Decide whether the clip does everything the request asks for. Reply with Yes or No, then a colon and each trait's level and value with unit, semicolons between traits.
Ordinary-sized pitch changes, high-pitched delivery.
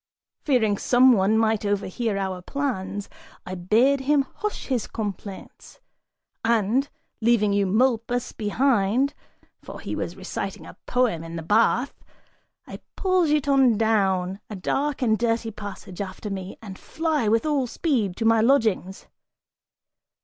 Yes: average, 4.7 semitones; high, 225 Hz